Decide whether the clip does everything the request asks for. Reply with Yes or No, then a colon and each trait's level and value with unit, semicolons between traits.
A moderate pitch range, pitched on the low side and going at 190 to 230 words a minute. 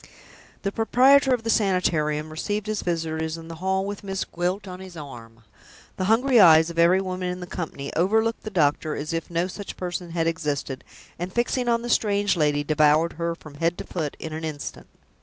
No: average, 4.1 semitones; medium, 175 Hz; average, 200 wpm